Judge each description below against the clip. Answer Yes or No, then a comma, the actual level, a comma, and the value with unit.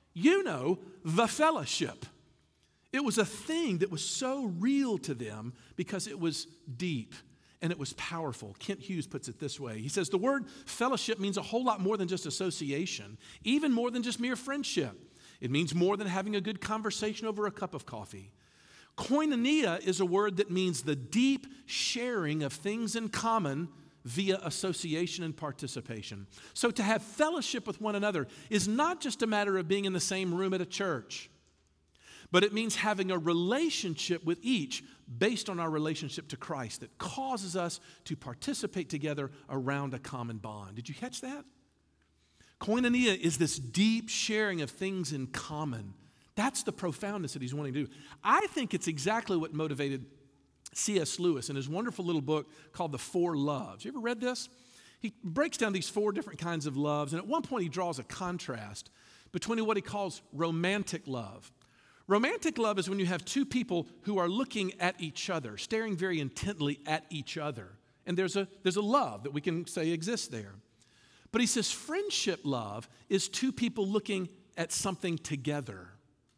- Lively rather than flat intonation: Yes, wide, 6.9 semitones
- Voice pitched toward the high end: No, medium, 180 Hz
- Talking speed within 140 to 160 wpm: No, average, 180 wpm